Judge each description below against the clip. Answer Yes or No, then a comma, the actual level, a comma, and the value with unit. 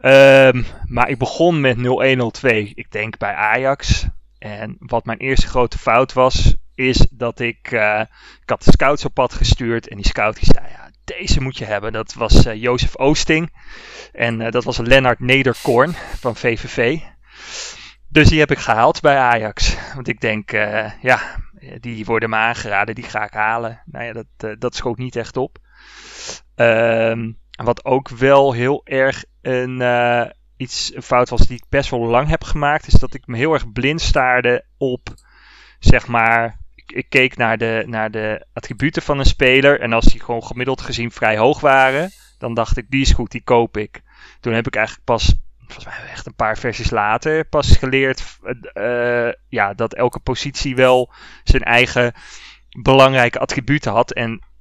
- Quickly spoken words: No, average, 180 wpm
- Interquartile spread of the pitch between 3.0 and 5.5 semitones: No, narrow, 2.6 semitones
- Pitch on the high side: No, low, 120 Hz